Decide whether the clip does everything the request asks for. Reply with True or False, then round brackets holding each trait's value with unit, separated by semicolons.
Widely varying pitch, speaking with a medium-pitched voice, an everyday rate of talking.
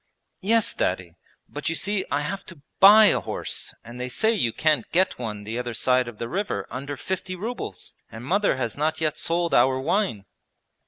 True (7.9 semitones; 145 Hz; 195 wpm)